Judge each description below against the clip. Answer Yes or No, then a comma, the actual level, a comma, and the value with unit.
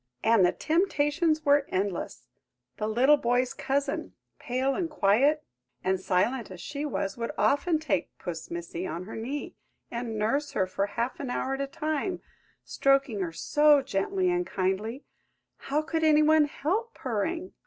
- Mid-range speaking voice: No, very high, 275 Hz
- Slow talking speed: No, average, 155 wpm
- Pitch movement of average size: No, wide, 6.2 semitones